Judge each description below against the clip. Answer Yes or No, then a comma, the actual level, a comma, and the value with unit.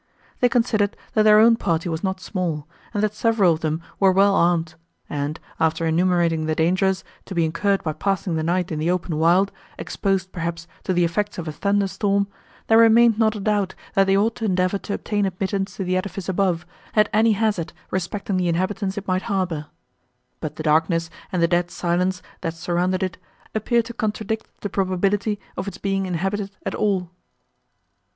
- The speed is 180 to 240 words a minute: Yes, average, 190 wpm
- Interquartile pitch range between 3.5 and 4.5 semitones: No, average, 3.1 semitones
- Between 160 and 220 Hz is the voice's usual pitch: Yes, high, 190 Hz